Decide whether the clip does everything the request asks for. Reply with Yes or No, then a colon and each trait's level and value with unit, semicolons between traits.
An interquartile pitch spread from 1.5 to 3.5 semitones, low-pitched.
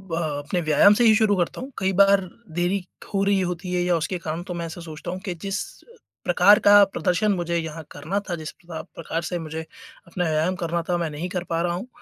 No: average, 2.7 semitones; medium, 175 Hz